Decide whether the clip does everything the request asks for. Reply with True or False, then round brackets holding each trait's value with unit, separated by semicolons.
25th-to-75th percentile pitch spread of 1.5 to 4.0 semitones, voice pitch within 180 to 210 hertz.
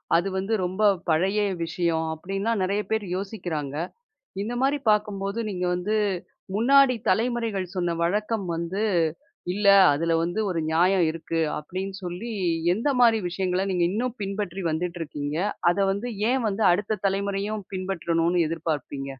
True (3.7 semitones; 190 Hz)